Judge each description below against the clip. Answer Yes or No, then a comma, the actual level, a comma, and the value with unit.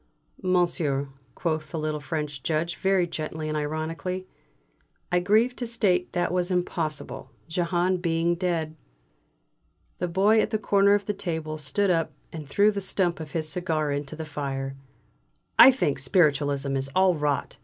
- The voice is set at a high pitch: No, medium, 165 Hz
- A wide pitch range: No, average, 3.3 semitones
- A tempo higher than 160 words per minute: No, average, 155 wpm